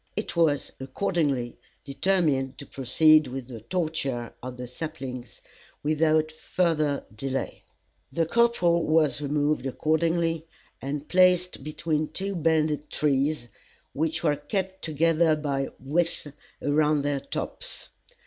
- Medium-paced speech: No, slow, 120 wpm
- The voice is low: No, medium, 155 Hz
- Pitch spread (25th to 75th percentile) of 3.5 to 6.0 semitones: No, average, 3.1 semitones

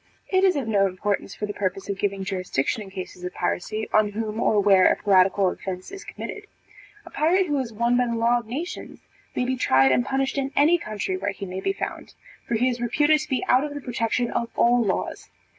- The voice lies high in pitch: Yes, high, 225 Hz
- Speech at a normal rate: No, fast, 230 wpm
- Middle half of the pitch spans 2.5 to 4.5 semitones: No, average, 5.1 semitones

